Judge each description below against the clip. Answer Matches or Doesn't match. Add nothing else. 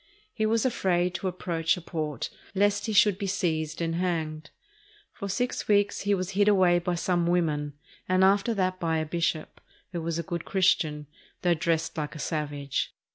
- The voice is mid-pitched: Matches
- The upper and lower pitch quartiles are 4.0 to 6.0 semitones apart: Doesn't match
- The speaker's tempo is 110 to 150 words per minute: Doesn't match